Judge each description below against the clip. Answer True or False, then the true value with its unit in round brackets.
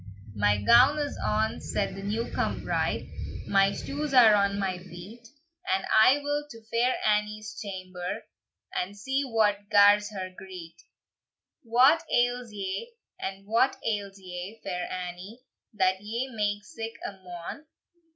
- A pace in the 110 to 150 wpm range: True (140 wpm)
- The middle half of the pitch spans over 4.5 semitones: False (3.7 semitones)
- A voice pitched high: True (210 Hz)